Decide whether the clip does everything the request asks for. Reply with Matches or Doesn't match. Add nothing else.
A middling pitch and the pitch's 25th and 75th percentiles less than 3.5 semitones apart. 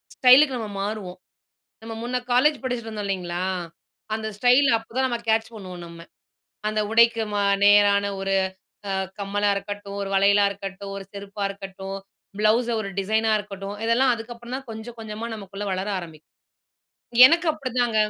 Doesn't match